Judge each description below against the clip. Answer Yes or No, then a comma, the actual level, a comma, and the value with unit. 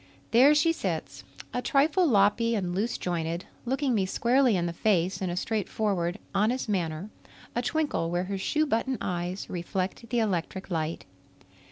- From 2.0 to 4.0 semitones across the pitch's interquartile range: No, wide, 5.4 semitones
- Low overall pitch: No, high, 205 Hz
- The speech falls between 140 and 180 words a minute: Yes, average, 160 wpm